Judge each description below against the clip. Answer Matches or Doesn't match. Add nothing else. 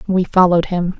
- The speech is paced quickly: Doesn't match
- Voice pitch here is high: Doesn't match